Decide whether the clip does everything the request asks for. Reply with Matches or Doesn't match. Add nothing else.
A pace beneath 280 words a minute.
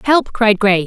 Matches